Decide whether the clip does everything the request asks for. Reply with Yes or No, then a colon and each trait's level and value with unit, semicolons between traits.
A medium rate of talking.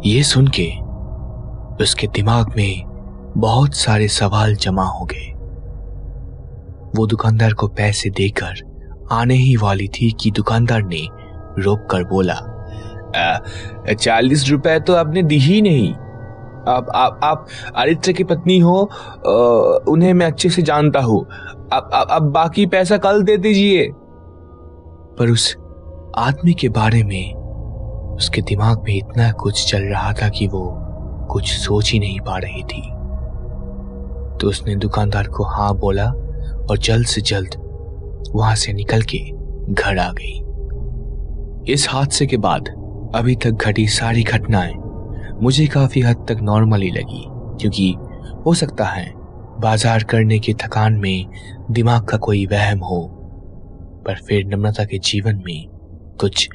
Yes: average, 135 wpm